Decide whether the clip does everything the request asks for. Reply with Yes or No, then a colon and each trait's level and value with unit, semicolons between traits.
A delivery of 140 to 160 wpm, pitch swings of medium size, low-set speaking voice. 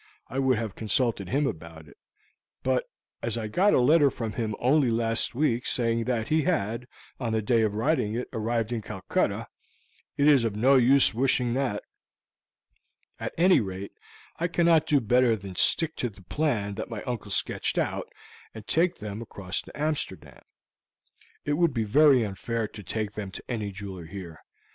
No: average, 175 wpm; average, 4.5 semitones; low, 115 Hz